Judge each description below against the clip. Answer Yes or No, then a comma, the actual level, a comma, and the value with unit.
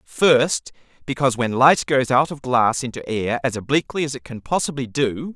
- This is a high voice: No, low, 135 Hz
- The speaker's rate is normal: Yes, average, 190 wpm